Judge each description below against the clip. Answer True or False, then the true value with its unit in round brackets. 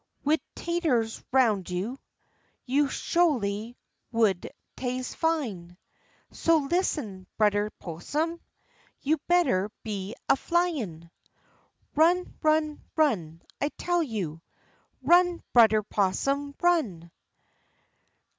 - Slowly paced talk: True (90 wpm)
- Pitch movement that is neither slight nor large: False (7.9 semitones)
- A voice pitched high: True (255 Hz)